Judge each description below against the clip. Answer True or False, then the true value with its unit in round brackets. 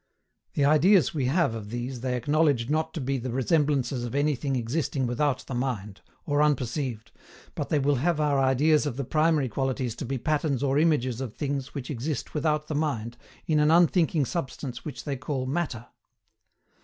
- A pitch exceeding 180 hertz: False (140 Hz)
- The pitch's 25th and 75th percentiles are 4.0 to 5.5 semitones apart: False (3.3 semitones)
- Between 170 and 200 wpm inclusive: True (180 wpm)